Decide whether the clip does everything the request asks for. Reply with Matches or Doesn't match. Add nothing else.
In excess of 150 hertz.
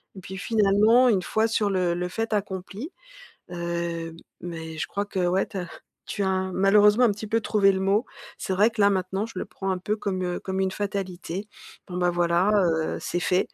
Matches